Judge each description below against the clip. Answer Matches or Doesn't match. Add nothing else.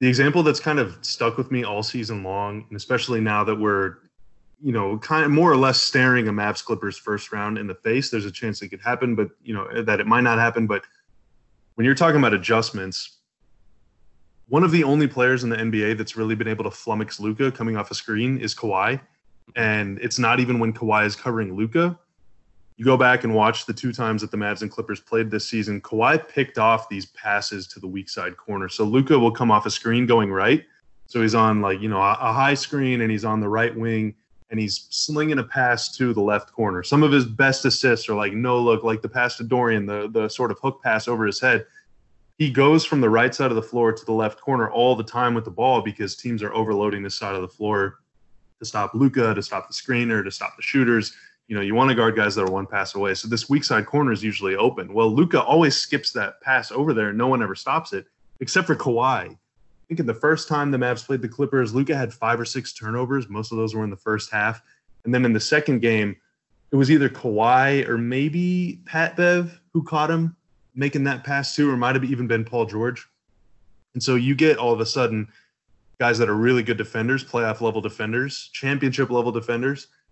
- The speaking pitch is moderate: Doesn't match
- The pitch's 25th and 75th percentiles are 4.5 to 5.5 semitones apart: Doesn't match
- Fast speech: Matches